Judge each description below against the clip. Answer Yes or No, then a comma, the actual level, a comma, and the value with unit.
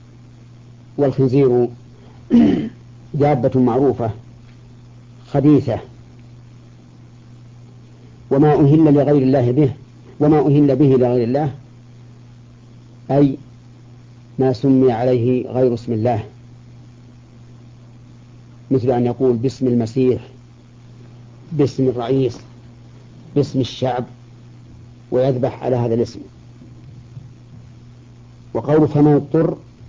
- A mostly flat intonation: Yes, narrow, 1.5 semitones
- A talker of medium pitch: No, low, 120 Hz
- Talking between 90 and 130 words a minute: No, average, 75 wpm